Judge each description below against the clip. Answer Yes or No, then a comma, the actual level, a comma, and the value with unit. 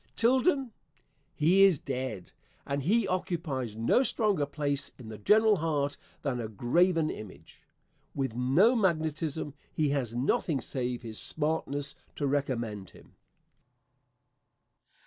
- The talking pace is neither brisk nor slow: No, slow, 120 wpm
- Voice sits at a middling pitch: Yes, medium, 145 Hz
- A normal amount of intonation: No, wide, 5.9 semitones